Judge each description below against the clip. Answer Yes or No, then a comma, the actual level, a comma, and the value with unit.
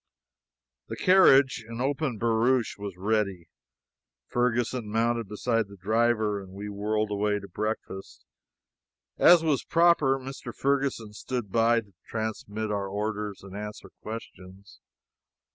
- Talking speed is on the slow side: Yes, slow, 125 wpm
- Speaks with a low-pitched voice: Yes, low, 110 Hz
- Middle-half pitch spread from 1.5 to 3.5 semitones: Yes, average, 3.1 semitones